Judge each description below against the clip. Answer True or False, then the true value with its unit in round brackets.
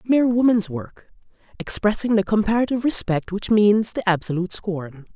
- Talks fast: False (140 wpm)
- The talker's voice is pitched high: True (205 Hz)